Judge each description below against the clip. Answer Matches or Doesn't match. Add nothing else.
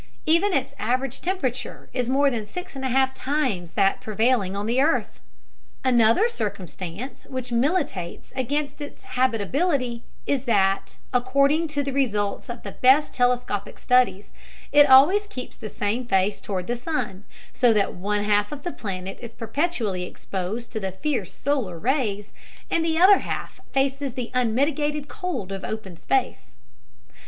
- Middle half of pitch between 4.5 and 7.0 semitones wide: Matches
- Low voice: Doesn't match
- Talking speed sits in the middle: Matches